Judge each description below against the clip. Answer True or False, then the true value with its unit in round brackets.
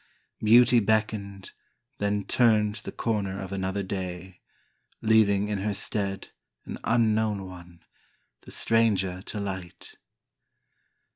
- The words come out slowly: True (110 wpm)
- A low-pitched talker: True (100 Hz)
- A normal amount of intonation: False (2.3 semitones)